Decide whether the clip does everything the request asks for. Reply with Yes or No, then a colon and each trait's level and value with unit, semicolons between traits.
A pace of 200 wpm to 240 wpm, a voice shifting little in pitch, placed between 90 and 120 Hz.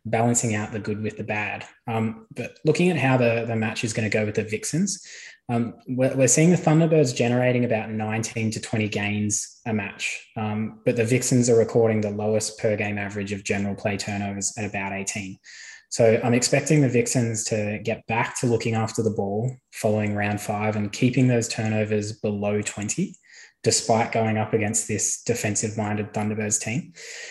No: average, 185 wpm; narrow, 2.3 semitones; low, 110 Hz